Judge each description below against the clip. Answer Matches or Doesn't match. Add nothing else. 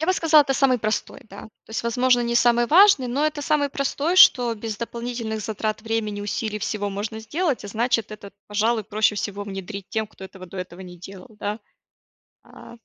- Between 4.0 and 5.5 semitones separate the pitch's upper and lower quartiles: Doesn't match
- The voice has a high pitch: Matches